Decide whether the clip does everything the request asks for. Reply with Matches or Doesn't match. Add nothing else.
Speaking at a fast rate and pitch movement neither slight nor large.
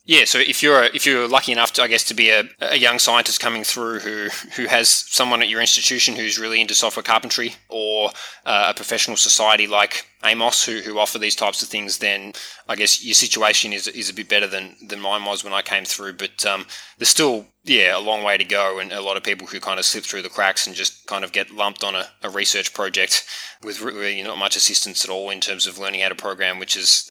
Doesn't match